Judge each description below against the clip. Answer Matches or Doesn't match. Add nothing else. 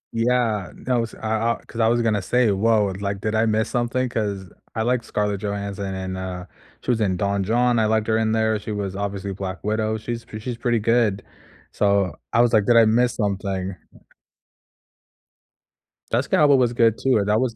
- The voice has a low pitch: Matches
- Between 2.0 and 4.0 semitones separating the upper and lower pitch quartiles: Matches